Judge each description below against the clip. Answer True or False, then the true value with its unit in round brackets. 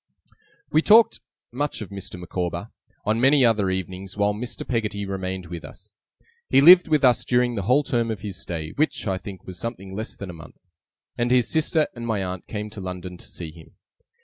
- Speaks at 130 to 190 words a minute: False (200 wpm)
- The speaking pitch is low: True (105 Hz)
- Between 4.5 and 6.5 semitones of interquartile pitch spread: True (4.8 semitones)